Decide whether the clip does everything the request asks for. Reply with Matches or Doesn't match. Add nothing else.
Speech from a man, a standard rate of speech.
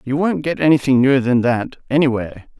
Matches